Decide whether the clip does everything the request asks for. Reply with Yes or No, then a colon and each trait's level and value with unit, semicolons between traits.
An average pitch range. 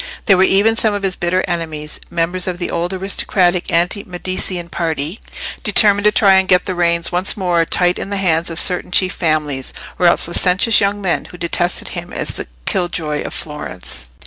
No: narrow, 2.1 semitones